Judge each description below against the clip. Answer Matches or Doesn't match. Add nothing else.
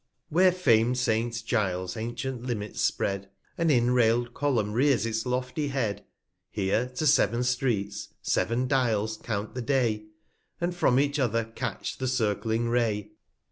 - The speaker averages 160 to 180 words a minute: Doesn't match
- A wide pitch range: Doesn't match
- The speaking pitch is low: Matches